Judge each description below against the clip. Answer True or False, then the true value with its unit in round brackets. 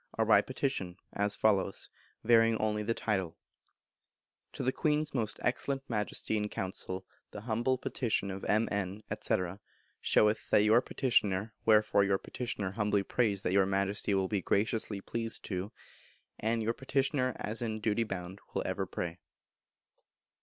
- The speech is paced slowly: False (145 wpm)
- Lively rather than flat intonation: False (2.7 semitones)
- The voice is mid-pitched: False (105 Hz)